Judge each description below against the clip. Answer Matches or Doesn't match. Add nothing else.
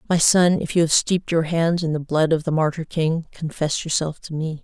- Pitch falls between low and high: Matches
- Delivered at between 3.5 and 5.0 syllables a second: Doesn't match